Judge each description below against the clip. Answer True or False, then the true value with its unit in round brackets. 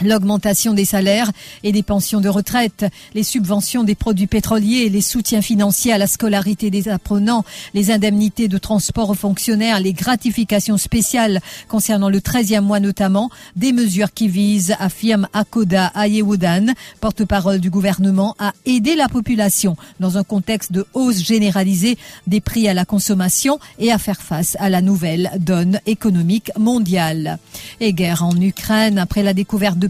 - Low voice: False (205 Hz)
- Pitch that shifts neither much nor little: False (2.0 semitones)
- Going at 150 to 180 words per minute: True (160 wpm)